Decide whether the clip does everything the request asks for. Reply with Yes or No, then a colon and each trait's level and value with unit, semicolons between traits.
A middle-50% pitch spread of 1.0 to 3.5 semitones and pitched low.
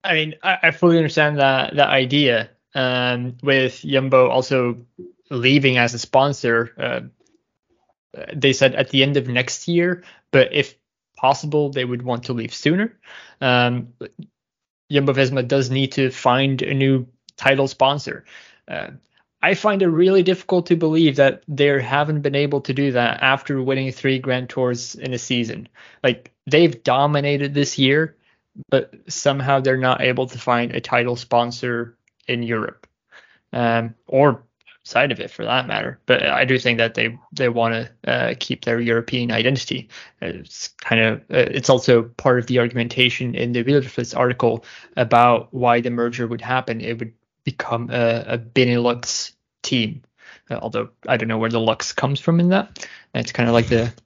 Yes: average, 2.8 semitones; low, 130 Hz